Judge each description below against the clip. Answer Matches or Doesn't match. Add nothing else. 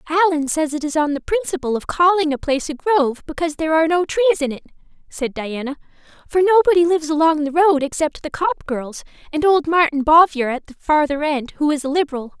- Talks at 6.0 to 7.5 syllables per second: Matches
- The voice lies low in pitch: Doesn't match